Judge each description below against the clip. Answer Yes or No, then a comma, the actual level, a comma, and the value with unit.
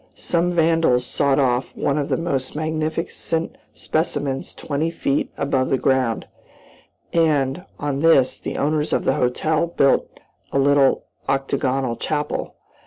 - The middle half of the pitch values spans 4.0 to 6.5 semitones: No, average, 3.0 semitones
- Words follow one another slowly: Yes, slow, 130 wpm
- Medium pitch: Yes, medium, 145 Hz